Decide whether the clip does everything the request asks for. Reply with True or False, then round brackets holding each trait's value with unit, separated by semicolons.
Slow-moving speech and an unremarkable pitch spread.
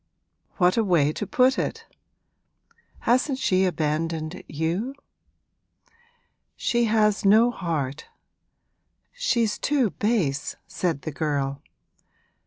False (95 wpm; 7.0 semitones)